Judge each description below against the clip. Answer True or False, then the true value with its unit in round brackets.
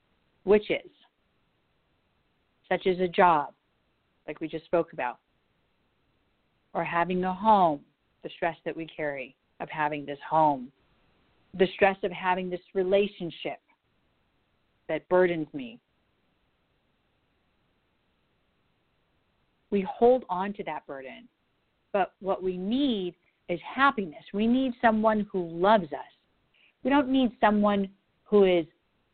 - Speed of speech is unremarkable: False (115 wpm)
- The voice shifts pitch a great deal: False (4.0 semitones)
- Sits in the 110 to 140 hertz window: False (185 Hz)